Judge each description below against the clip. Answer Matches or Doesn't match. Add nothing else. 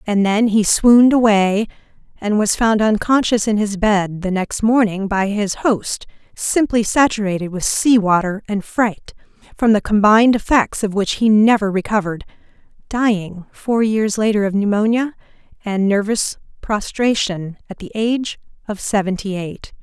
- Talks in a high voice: Matches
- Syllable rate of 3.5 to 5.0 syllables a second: Matches